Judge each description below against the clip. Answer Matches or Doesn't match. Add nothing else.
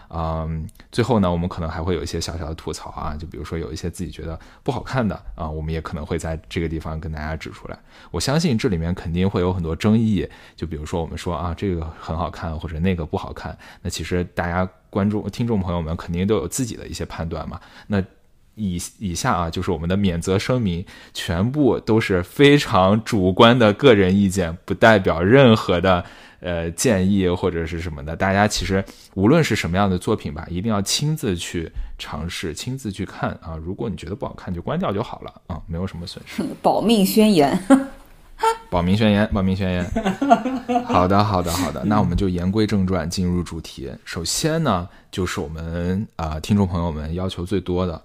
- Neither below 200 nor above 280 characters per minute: Doesn't match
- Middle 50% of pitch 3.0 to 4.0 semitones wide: Matches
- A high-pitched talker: Doesn't match